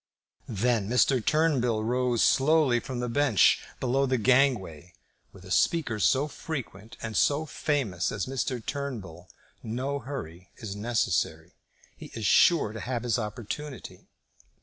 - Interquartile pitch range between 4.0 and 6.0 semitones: Yes, average, 4.3 semitones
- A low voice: Yes, low, 120 Hz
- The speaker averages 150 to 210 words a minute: No, slow, 135 wpm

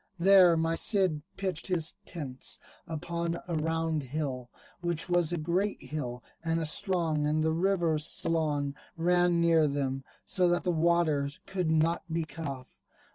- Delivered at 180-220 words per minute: No, average, 155 wpm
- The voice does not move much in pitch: Yes, narrow, 2.3 semitones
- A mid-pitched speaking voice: Yes, medium, 165 Hz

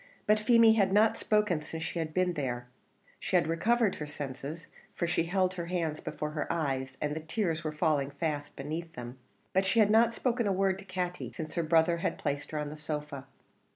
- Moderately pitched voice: Yes, medium, 165 Hz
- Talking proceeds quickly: Yes, fast, 215 wpm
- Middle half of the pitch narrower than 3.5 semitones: No, average, 4.2 semitones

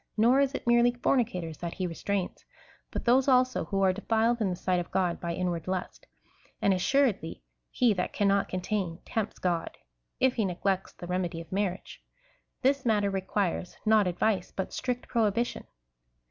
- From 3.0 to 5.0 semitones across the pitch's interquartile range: Yes, average, 4.6 semitones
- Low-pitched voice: No, high, 195 Hz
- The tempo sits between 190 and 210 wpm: No, average, 170 wpm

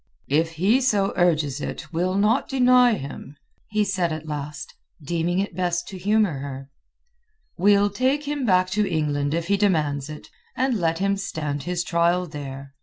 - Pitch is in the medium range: Yes, medium, 175 Hz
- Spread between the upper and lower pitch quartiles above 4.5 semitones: Yes, average, 5.1 semitones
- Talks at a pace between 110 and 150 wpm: No, average, 170 wpm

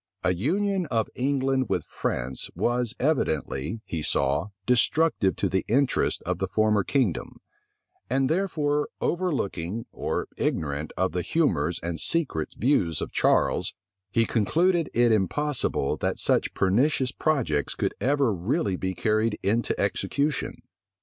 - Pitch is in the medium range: No, low, 115 Hz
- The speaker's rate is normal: No, slow, 130 wpm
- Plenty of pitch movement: Yes, wide, 7.7 semitones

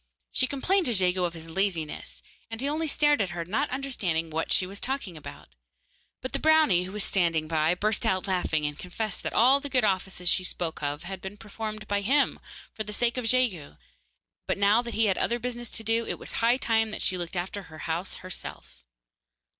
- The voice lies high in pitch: Yes, high, 200 Hz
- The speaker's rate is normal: No, fast, 215 wpm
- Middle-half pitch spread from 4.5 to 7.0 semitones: Yes, average, 5.2 semitones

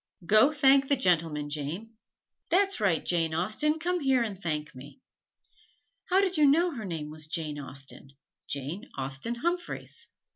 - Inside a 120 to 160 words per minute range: Yes, average, 150 wpm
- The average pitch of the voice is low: No, high, 200 Hz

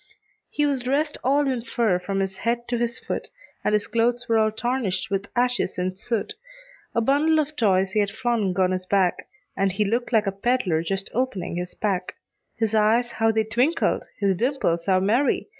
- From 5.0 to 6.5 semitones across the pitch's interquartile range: No, average, 4.1 semitones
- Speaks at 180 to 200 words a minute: Yes, average, 195 wpm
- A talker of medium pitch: No, high, 220 Hz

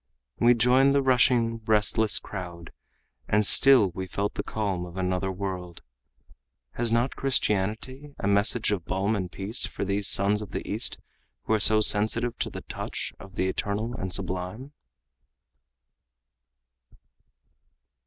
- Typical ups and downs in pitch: Yes, average, 3.7 semitones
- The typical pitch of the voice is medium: No, low, 105 Hz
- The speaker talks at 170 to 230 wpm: No, average, 140 wpm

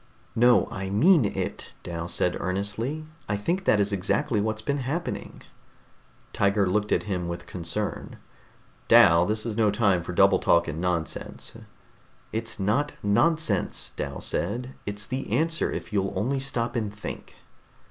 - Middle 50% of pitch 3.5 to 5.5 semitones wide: Yes, average, 4.5 semitones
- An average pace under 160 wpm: Yes, average, 150 wpm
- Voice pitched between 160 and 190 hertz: No, low, 105 Hz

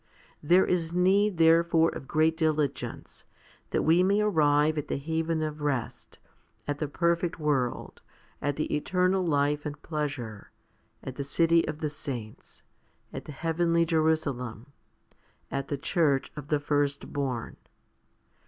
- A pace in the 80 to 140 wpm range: Yes, slow, 135 wpm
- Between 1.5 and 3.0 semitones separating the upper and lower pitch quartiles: Yes, average, 2.7 semitones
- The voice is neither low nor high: Yes, medium, 155 Hz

